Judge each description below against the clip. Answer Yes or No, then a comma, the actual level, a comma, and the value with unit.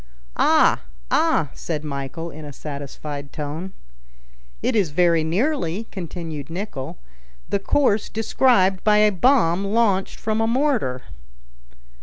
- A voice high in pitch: No, medium, 180 Hz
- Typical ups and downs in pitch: No, wide, 6.0 semitones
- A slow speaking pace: Yes, slow, 120 wpm